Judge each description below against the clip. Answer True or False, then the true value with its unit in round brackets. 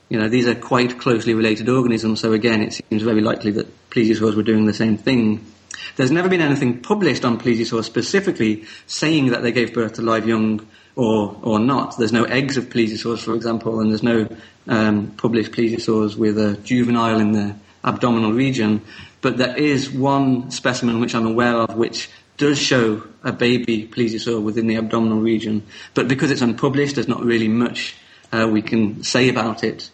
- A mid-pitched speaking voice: False (115 Hz)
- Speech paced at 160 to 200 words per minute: True (185 wpm)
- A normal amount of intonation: False (2.0 semitones)